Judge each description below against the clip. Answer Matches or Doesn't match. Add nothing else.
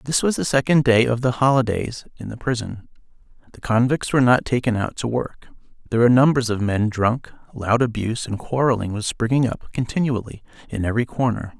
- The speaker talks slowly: Doesn't match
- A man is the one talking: Matches